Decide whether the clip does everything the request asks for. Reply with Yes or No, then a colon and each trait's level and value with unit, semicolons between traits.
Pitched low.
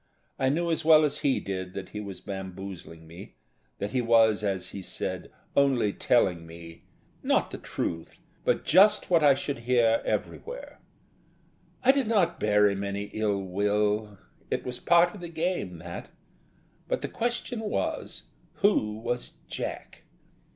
Yes: low, 110 Hz